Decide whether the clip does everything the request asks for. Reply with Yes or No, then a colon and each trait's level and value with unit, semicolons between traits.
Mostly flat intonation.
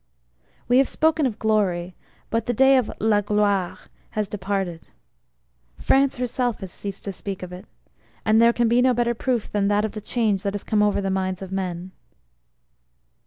No: average, 3.6 semitones